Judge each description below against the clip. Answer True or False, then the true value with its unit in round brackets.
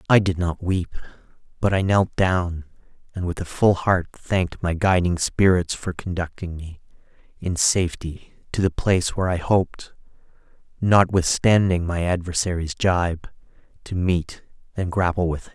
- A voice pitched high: False (90 Hz)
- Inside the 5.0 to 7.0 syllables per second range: False (4.7 syllables/s)